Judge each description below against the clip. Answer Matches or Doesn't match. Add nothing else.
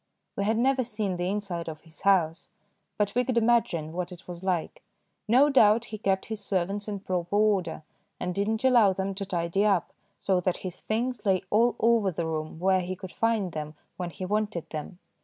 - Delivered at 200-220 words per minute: Matches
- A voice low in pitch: Doesn't match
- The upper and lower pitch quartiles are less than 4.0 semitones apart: Matches